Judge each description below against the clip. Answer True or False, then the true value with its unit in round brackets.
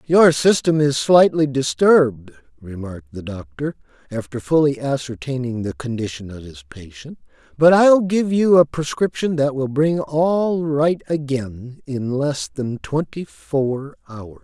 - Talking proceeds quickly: False (140 wpm)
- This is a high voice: False (140 Hz)